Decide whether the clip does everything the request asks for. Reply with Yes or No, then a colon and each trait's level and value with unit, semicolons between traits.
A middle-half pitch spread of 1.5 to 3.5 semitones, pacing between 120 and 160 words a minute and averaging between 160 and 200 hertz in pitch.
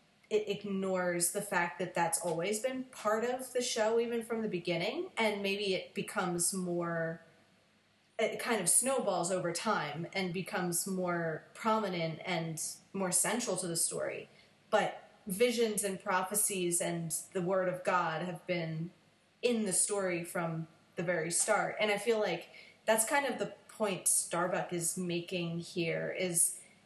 Yes: average, 3.2 semitones; average, 155 wpm; medium, 185 Hz